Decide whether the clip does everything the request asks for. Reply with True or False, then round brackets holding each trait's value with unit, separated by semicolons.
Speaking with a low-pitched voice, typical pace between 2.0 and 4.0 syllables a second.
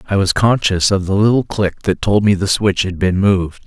False (100 Hz; 5.2 syllables/s)